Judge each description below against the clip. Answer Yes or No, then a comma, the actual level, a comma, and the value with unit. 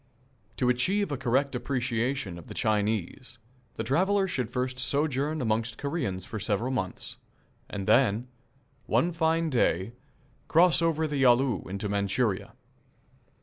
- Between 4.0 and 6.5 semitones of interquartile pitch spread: Yes, average, 5.1 semitones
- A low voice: Yes, low, 125 Hz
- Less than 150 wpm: Yes, slow, 135 wpm